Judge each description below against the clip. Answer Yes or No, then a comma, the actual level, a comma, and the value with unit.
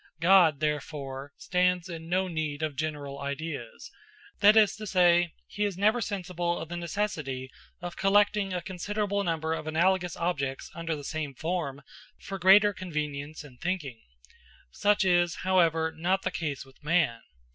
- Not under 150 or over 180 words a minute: Yes, average, 155 wpm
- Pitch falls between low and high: Yes, medium, 170 Hz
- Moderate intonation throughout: Yes, average, 4.0 semitones